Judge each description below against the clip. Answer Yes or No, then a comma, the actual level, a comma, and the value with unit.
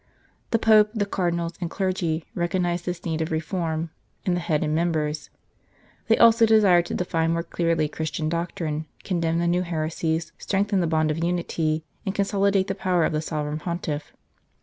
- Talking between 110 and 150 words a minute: No, average, 170 wpm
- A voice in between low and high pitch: Yes, medium, 170 Hz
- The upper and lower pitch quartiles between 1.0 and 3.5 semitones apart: Yes, average, 2.7 semitones